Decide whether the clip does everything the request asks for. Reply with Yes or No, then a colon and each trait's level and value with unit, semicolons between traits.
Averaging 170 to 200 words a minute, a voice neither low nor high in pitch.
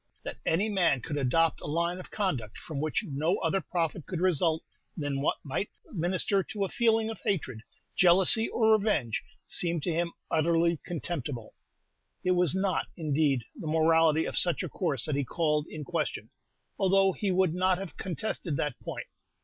Yes: average, 175 wpm; medium, 170 Hz